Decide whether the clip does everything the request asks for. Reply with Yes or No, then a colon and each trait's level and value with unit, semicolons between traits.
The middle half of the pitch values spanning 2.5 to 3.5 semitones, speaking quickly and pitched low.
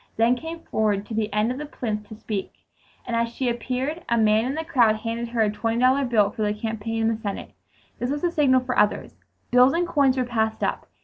No: average, 3.0 semitones; fast, 240 wpm; high, 235 Hz